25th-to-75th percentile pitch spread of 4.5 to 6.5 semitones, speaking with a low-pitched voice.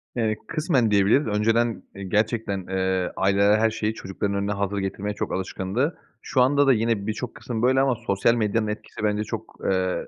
No: average, 2.9 semitones; low, 105 Hz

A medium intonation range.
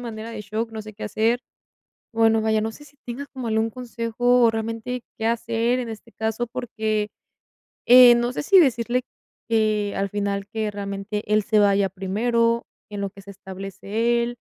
No: narrow, 2.3 semitones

